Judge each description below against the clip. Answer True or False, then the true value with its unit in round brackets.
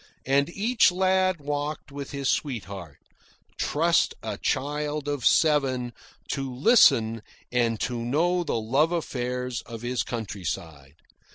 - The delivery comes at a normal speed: False (120 wpm)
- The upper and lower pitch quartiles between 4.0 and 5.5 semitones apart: True (4.3 semitones)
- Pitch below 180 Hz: True (135 Hz)